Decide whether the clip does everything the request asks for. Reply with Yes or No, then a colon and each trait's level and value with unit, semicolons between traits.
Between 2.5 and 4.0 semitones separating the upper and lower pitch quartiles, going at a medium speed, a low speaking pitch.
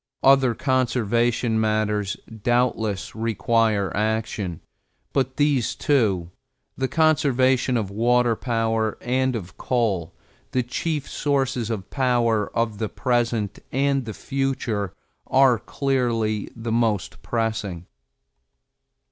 No: average, 3.1 semitones; slow, 105 wpm; low, 115 Hz